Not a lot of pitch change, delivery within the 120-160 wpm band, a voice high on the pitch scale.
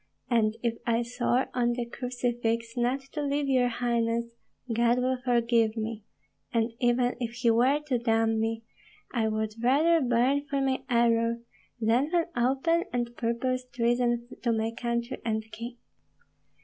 Yes: narrow, 1.6 semitones; average, 150 wpm; high, 240 Hz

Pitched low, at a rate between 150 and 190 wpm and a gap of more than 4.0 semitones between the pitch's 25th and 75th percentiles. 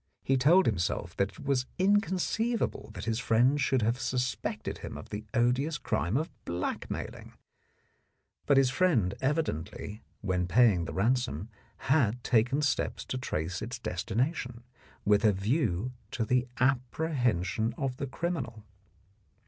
No: low, 125 Hz; average, 140 wpm; average, 4.7 semitones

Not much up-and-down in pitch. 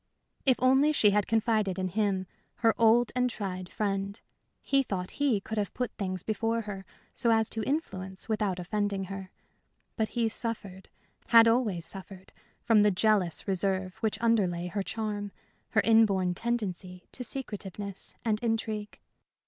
No: average, 3.0 semitones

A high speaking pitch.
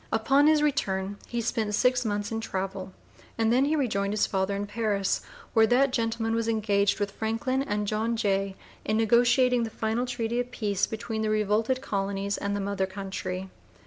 Yes: high, 220 Hz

